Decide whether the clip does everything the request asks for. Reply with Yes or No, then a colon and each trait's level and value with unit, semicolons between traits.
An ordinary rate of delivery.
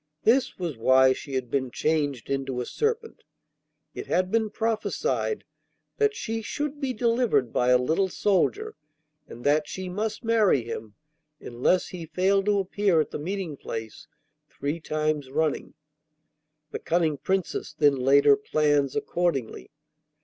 Yes: average, 145 wpm